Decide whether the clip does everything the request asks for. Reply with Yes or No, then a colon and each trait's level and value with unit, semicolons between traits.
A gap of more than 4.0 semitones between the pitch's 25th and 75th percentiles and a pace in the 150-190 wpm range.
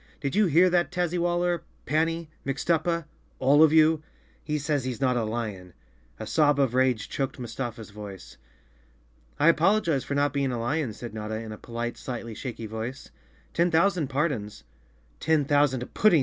Yes: wide, 5.5 semitones; average, 160 wpm